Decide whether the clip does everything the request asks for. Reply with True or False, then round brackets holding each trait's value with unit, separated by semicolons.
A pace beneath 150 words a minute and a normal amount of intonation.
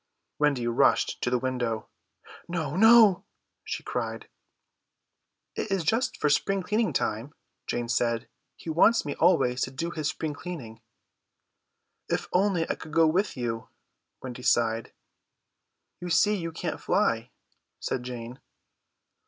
False (135 wpm; 6.6 semitones)